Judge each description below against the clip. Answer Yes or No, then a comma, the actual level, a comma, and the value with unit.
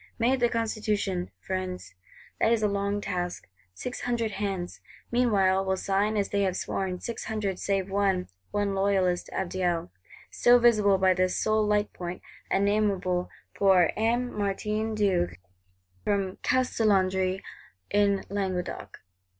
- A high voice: Yes, high, 200 Hz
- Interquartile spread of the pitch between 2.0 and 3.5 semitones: Yes, narrow, 2.4 semitones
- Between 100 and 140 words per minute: Yes, slow, 135 wpm